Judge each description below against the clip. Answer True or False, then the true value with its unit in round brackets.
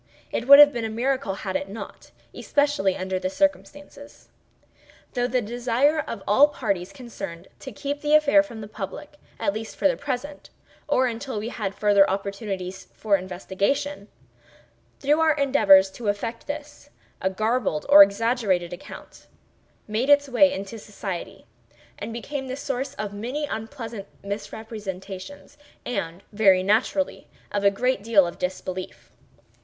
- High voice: True (220 Hz)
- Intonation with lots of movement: True (5.8 semitones)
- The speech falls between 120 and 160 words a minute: True (140 wpm)